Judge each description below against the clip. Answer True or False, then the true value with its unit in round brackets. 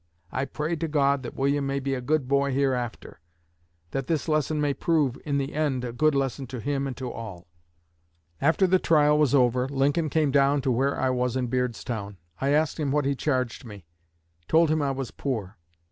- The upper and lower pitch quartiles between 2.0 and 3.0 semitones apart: True (2.7 semitones)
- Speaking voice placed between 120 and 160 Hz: True (140 Hz)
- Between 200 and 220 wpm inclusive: True (205 wpm)